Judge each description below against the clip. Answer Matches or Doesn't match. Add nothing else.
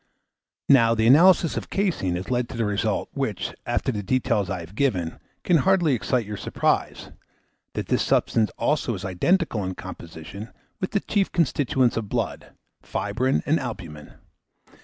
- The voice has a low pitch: Matches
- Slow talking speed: Doesn't match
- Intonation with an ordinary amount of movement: Doesn't match